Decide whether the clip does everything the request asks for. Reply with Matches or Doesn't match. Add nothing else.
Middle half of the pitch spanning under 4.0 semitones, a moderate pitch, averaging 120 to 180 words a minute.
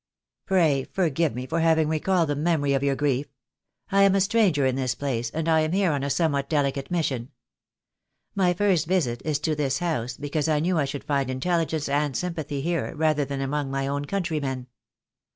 Doesn't match